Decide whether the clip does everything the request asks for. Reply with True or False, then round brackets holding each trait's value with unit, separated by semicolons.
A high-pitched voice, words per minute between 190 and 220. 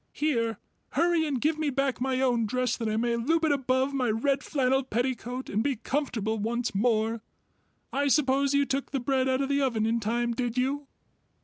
True (255 Hz; 200 wpm)